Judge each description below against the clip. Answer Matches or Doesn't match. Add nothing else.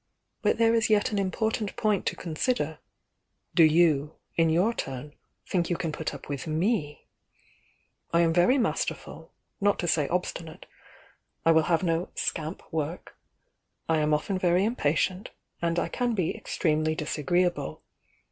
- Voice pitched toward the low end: Doesn't match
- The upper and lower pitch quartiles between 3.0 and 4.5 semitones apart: Matches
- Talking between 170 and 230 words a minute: Doesn't match